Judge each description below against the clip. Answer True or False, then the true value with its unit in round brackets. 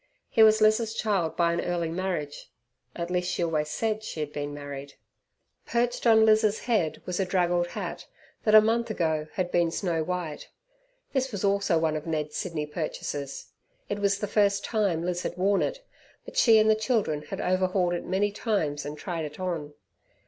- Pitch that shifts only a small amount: False (5.1 semitones)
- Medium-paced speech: True (190 wpm)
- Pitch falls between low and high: True (180 Hz)